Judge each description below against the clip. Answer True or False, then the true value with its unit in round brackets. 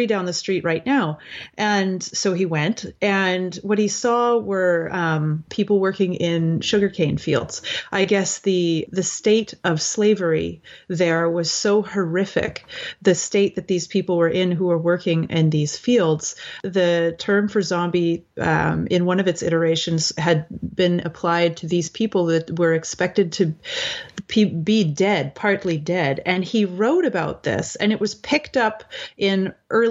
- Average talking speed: True (160 wpm)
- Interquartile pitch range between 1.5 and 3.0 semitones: False (3.4 semitones)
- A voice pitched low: False (185 Hz)